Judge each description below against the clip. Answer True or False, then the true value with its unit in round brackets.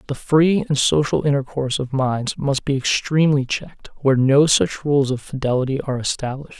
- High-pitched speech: False (140 Hz)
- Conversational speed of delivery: True (175 wpm)